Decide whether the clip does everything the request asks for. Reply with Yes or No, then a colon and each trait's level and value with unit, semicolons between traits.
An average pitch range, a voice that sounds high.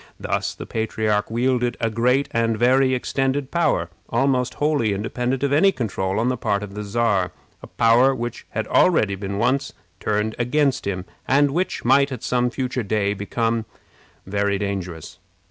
No: average, 4.2 semitones; low, 115 Hz